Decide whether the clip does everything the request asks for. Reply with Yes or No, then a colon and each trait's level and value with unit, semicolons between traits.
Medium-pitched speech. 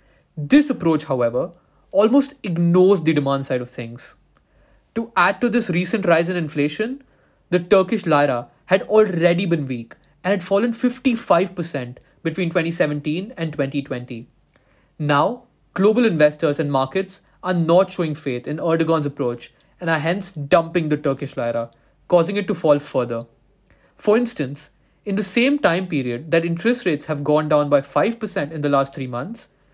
Yes: medium, 165 Hz